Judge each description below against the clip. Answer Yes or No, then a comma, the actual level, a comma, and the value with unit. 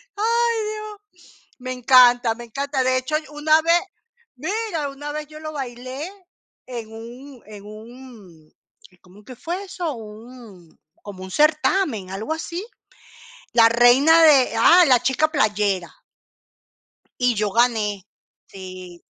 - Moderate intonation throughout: No, wide, 6.0 semitones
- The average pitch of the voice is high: Yes, very high, 255 Hz